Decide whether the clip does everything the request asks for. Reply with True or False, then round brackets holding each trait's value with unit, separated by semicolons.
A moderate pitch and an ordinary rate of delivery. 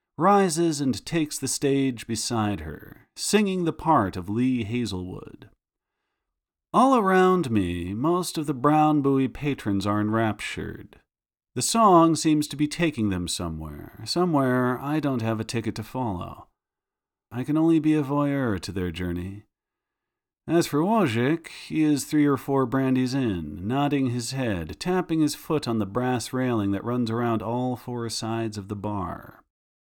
False (125 Hz; 155 wpm)